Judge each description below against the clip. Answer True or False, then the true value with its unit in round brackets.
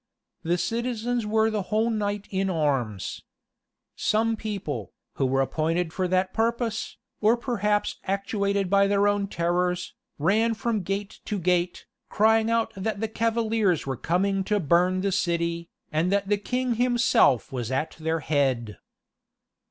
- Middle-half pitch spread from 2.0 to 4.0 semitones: False (4.5 semitones)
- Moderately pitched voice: False (200 Hz)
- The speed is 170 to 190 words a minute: False (145 wpm)